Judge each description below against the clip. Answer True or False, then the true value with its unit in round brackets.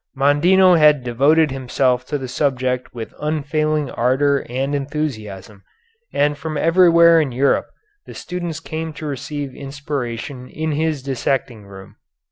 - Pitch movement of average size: True (3.4 semitones)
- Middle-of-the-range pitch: True (145 Hz)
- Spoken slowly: True (130 wpm)